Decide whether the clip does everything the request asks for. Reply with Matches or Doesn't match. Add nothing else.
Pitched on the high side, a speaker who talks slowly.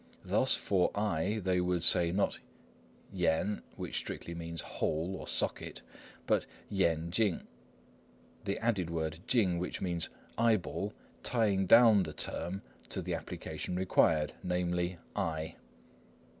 Doesn't match